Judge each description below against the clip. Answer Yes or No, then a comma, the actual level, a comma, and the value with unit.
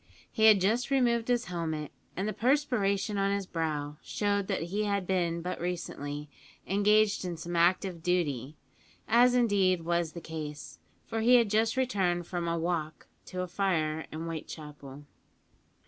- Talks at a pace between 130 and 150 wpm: No, average, 160 wpm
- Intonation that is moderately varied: Yes, average, 4.4 semitones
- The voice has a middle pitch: Yes, medium, 180 Hz